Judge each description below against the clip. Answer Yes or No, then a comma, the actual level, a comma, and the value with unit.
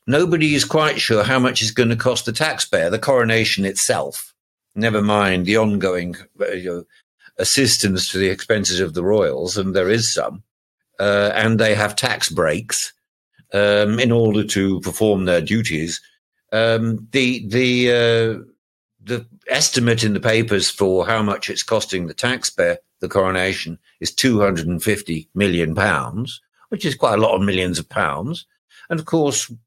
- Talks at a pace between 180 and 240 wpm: No, average, 165 wpm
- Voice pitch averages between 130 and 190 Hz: No, low, 110 Hz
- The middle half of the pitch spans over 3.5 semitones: Yes, average, 4.0 semitones